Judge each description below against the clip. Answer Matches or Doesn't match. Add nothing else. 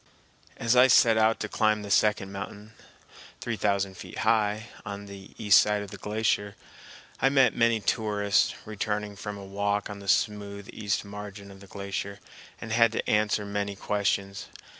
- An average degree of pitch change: Doesn't match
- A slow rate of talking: Doesn't match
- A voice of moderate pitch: Doesn't match